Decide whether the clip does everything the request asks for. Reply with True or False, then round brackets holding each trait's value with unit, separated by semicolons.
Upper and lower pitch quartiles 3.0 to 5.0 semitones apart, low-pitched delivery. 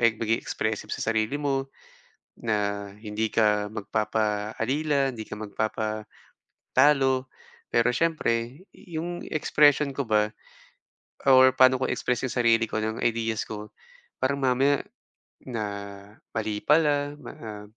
True (4.1 semitones; 115 Hz)